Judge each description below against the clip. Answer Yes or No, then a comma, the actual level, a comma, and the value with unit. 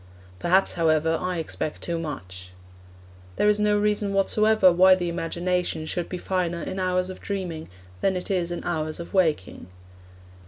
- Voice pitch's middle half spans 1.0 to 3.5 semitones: Yes, narrow, 2.5 semitones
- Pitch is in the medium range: Yes, medium, 180 Hz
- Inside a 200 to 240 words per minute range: No, average, 155 wpm